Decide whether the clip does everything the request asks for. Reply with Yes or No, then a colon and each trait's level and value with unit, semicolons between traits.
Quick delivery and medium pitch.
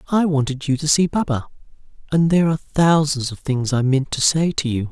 Yes: fast, 220 wpm; medium, 145 Hz